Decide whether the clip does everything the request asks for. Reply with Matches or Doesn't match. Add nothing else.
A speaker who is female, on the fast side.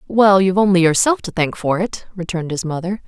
Matches